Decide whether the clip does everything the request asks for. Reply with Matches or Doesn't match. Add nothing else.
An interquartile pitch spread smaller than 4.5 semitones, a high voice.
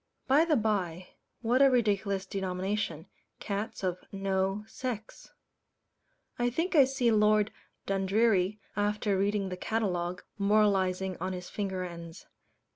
Matches